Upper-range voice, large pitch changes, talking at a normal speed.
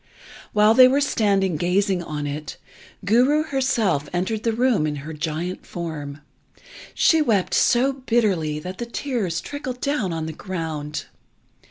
Yes: high, 195 Hz; wide, 7.4 semitones; average, 145 wpm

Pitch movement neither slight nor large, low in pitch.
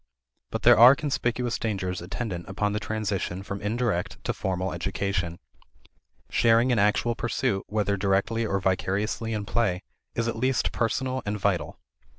Yes: average, 3.3 semitones; low, 105 Hz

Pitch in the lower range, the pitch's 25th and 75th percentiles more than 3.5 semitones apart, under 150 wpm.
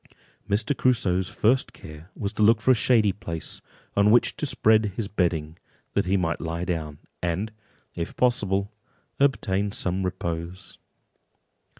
Yes: low, 100 Hz; average, 4.3 semitones; average, 140 wpm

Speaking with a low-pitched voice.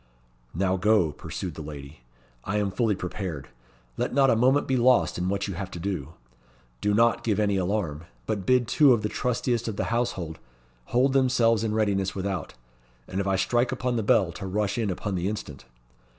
Yes: low, 105 Hz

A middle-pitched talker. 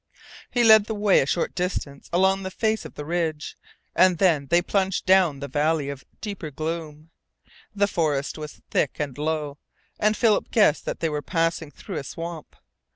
Yes: medium, 165 Hz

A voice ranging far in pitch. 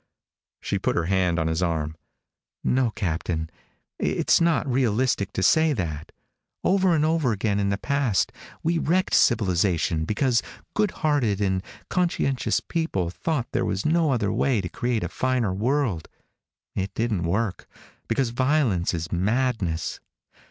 Yes: wide, 7.1 semitones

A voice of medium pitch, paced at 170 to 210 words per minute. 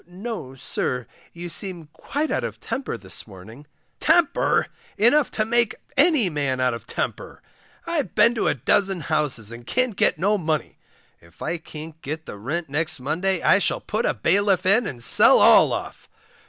Yes: medium, 170 Hz; average, 175 wpm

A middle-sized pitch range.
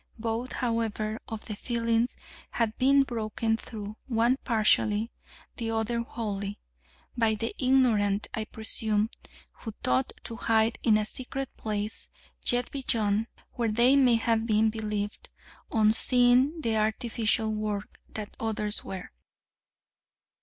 No: narrow, 1.9 semitones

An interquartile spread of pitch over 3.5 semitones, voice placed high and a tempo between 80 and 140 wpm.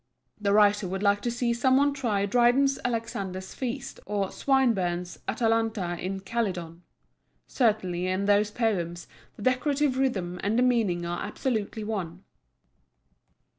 Yes: average, 4.4 semitones; high, 210 Hz; slow, 135 wpm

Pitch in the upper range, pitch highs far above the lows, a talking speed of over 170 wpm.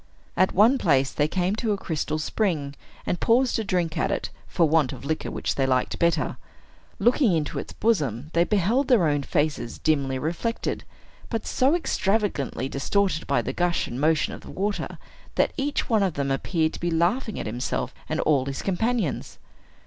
No: medium, 170 Hz; wide, 6.3 semitones; average, 185 wpm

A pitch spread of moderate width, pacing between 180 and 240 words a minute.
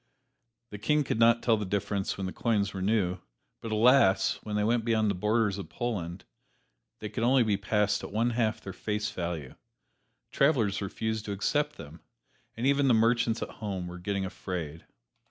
Yes: average, 3.1 semitones; average, 185 wpm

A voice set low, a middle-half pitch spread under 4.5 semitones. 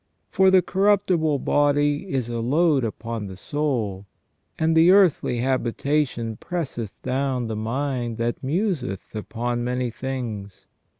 No: low, 130 Hz; average, 4.8 semitones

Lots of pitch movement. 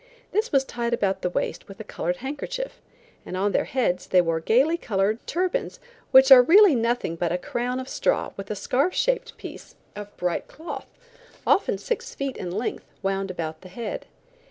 Yes: wide, 6.5 semitones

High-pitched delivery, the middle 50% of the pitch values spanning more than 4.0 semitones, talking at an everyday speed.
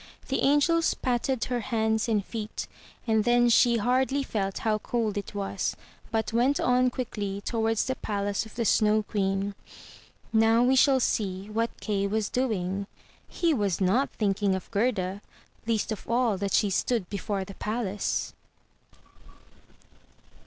No: high, 220 Hz; average, 3.3 semitones; average, 150 wpm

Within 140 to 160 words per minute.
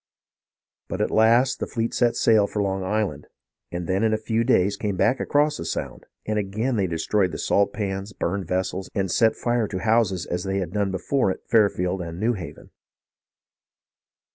No: average, 190 wpm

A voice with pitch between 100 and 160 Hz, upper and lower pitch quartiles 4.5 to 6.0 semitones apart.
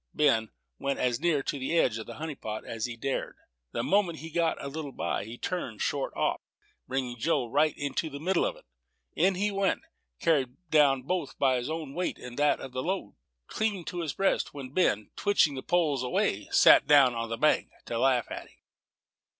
Yes: medium, 140 Hz; average, 4.8 semitones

